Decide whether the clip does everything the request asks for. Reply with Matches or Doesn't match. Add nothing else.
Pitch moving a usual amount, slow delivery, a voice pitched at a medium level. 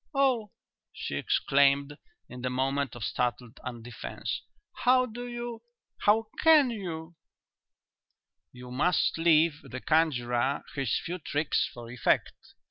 Doesn't match